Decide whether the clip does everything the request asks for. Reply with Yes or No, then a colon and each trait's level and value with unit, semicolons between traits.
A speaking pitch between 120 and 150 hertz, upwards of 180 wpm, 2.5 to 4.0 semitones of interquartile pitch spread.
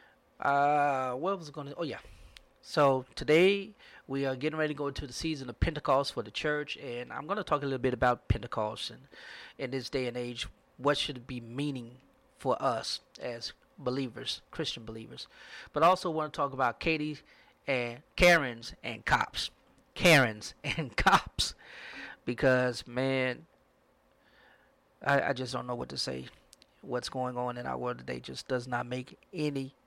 No: low, 135 Hz; average, 170 wpm; average, 3.7 semitones